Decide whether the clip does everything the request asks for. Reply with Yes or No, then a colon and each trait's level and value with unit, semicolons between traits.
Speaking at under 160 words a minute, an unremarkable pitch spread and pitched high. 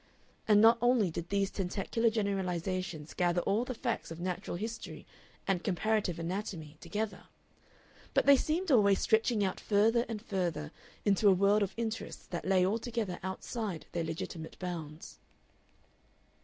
Yes: average, 140 wpm; average, 3.9 semitones; high, 195 Hz